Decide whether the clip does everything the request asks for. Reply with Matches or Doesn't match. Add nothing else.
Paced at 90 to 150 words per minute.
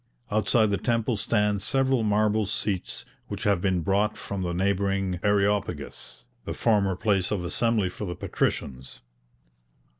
Matches